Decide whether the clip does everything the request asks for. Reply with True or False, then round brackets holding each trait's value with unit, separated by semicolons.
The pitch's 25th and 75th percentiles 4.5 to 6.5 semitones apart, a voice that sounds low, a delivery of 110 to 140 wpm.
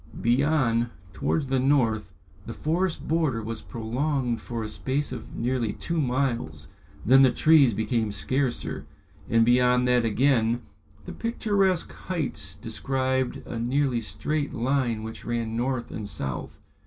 False (3.5 semitones; 125 Hz; 135 wpm)